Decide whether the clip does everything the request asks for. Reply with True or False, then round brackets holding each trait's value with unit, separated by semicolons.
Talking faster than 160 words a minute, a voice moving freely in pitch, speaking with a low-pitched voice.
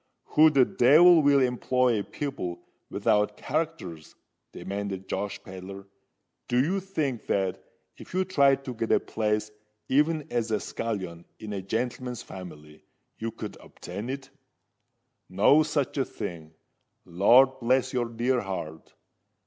False (135 wpm; 5.8 semitones; 120 Hz)